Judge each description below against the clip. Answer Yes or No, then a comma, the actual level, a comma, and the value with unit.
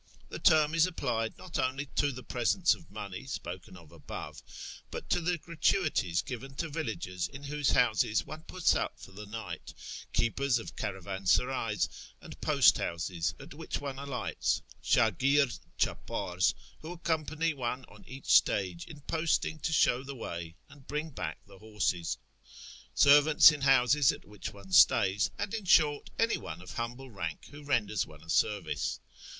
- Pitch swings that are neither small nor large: No, wide, 7.1 semitones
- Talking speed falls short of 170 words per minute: Yes, average, 160 wpm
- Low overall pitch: Yes, low, 125 Hz